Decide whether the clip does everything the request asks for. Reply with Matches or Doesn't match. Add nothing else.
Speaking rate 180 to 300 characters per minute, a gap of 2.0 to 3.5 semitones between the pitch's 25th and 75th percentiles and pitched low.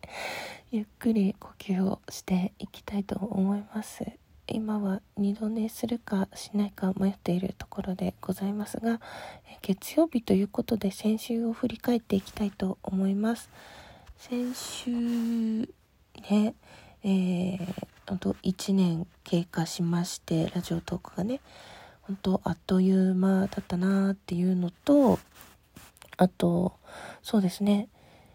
Doesn't match